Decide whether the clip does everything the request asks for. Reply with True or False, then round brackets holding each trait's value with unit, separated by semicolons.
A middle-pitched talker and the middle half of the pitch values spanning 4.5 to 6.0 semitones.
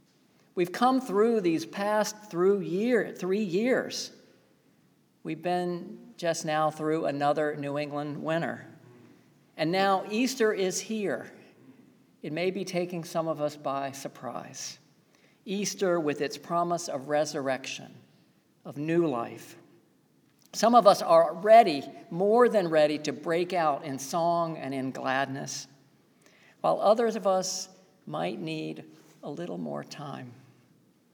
True (170 Hz; 5.2 semitones)